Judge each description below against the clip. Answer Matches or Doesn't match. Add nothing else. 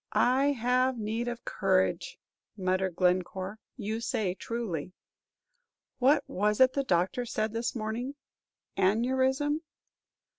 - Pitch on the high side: Matches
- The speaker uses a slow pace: Matches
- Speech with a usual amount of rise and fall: Matches